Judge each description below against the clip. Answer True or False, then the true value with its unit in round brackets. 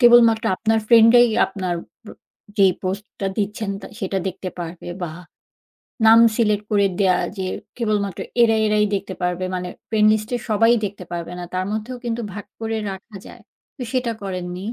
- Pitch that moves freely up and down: False (3.2 semitones)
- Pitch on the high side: True (205 Hz)